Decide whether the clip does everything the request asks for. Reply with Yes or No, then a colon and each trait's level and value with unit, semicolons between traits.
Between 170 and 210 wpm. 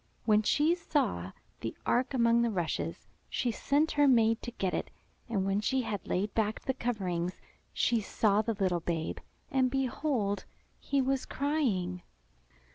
No: average, 155 wpm